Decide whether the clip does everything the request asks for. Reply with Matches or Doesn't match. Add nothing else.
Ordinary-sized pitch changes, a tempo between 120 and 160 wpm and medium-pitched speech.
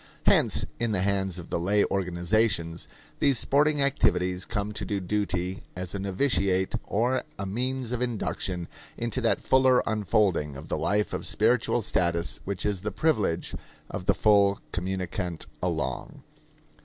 Doesn't match